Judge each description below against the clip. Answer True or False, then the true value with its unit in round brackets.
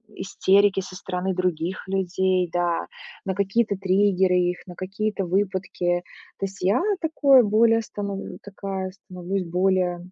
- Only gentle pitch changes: True (1.7 semitones)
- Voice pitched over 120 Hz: True (190 Hz)